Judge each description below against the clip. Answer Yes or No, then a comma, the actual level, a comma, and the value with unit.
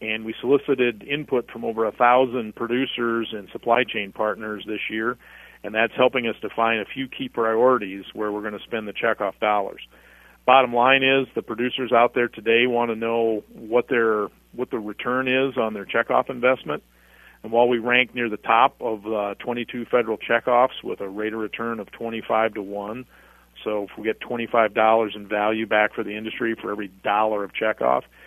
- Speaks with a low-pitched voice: Yes, low, 115 Hz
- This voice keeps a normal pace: Yes, average, 195 wpm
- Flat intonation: Yes, narrow, 2.3 semitones